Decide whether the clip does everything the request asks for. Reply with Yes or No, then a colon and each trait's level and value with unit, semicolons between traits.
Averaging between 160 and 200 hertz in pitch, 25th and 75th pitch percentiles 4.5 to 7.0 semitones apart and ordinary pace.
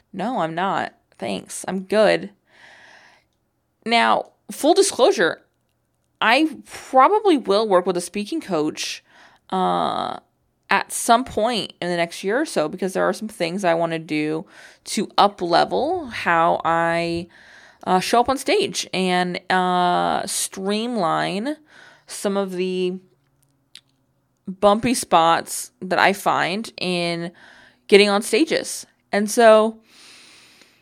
No: high, 190 Hz; average, 4.8 semitones; slow, 125 wpm